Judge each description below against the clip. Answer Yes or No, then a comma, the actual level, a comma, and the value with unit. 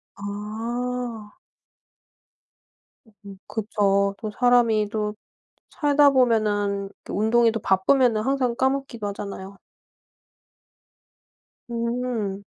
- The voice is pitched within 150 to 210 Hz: No, high, 220 Hz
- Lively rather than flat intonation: No, average, 3.2 semitones